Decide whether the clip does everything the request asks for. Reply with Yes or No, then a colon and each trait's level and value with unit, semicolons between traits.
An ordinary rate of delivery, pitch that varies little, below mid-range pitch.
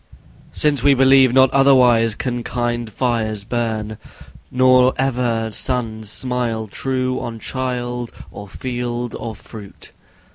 No: slow, 115 wpm; narrow, 2.3 semitones; low, 120 Hz